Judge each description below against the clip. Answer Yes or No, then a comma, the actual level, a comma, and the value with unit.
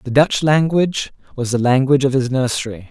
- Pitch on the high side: No, low, 135 Hz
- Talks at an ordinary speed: Yes, average, 185 wpm